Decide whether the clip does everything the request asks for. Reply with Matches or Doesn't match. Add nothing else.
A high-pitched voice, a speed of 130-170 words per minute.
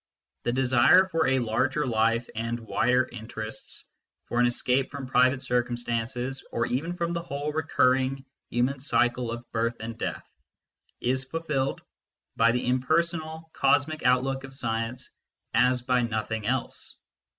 Doesn't match